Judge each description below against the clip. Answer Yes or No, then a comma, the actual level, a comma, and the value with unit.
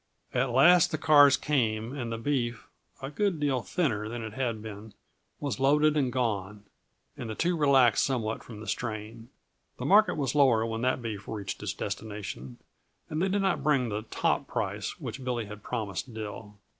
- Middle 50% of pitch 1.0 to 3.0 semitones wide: No, average, 4.6 semitones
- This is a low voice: Yes, low, 120 Hz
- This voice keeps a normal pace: Yes, average, 180 wpm